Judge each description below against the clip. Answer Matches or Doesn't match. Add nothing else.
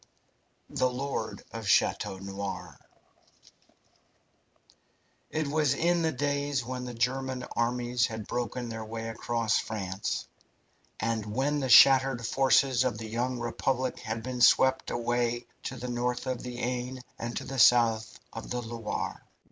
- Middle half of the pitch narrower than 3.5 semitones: Matches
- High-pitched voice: Doesn't match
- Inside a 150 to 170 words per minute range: Doesn't match